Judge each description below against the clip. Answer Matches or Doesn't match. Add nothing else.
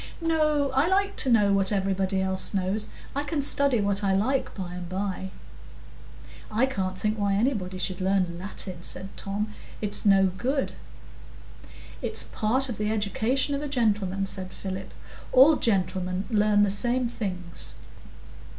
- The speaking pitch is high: Matches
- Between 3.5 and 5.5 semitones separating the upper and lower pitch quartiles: Matches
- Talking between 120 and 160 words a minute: Matches